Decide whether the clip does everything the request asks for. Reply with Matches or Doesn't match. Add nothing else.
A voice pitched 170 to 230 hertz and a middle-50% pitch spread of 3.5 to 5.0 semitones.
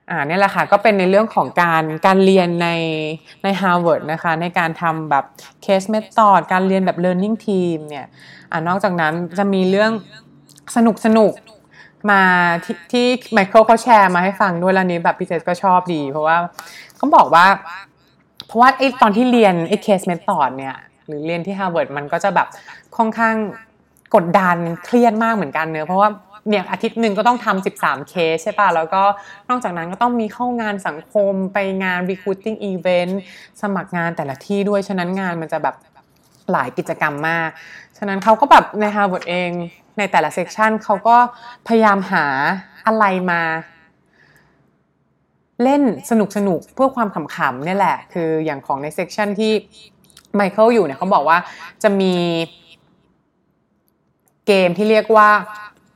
Matches